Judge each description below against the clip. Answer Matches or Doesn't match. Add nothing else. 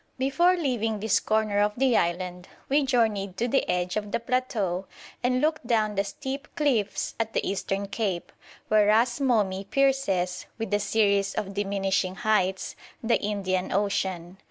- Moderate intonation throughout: Matches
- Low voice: Doesn't match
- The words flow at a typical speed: Matches